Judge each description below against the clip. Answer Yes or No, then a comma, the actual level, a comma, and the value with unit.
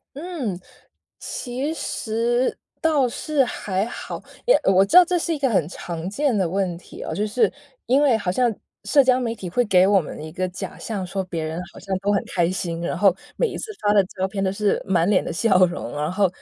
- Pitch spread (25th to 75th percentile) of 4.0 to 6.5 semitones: Yes, average, 5.3 semitones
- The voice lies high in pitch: Yes, high, 200 Hz